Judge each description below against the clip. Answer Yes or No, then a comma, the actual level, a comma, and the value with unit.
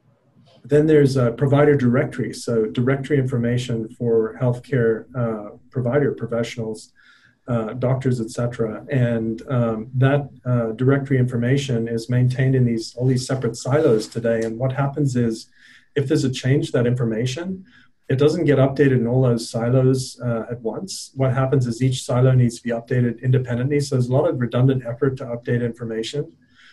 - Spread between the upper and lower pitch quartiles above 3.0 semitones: No, narrow, 2.4 semitones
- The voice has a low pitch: Yes, low, 125 Hz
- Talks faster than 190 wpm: No, average, 165 wpm